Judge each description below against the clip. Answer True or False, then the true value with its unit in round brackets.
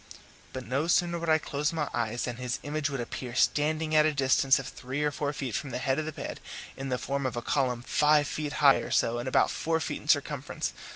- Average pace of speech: False (245 wpm)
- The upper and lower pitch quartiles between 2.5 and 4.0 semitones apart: True (3.0 semitones)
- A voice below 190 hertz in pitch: True (140 Hz)